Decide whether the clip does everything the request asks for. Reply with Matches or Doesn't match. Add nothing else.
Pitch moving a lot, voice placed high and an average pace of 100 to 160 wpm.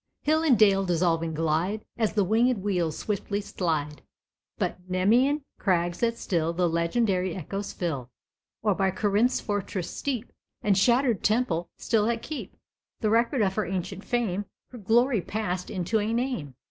Doesn't match